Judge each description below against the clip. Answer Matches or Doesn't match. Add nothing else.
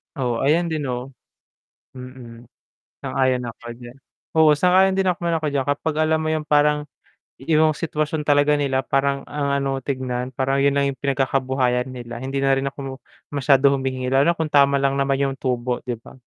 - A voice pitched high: Doesn't match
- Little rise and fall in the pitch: Matches